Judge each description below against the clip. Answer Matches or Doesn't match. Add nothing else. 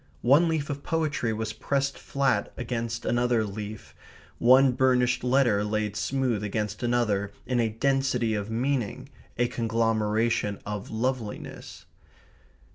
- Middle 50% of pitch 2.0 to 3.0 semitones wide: Doesn't match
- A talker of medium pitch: Doesn't match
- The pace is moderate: Doesn't match